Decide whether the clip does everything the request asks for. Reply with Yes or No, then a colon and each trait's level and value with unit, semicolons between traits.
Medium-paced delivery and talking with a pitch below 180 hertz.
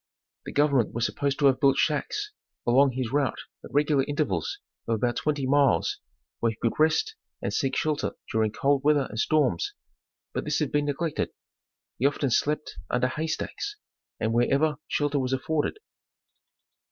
Yes: average, 165 wpm; medium, 140 Hz